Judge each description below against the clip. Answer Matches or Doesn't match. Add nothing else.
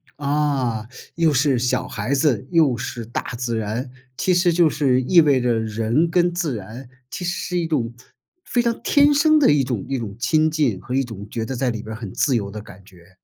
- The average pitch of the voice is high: Doesn't match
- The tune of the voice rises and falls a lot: Matches